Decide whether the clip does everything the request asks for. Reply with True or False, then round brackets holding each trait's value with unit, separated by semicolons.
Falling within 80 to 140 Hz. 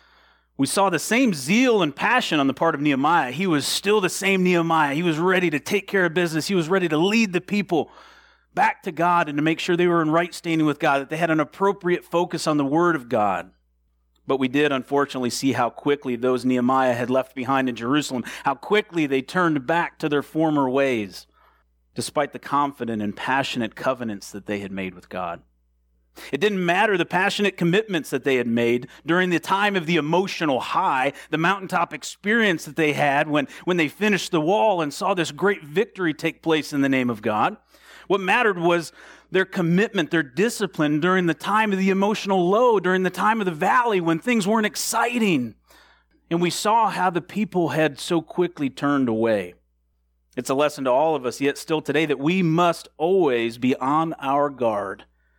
False (160 Hz)